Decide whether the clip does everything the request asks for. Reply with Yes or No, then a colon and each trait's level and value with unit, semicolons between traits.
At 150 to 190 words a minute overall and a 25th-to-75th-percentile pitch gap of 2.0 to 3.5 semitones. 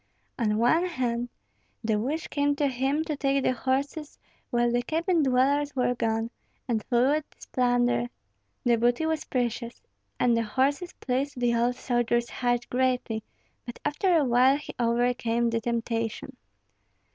Yes: average, 155 wpm; average, 3.0 semitones